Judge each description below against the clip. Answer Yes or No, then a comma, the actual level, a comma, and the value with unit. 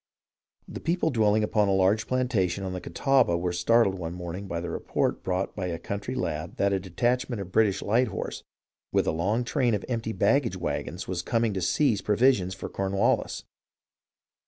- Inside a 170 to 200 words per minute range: Yes, average, 180 wpm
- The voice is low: Yes, low, 100 Hz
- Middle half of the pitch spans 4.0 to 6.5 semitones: Yes, average, 4.3 semitones